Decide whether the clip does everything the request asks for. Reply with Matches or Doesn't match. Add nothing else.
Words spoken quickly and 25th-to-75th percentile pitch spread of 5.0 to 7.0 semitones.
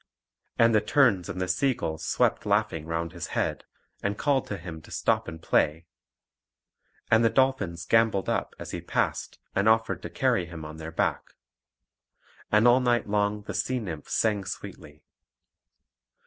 Doesn't match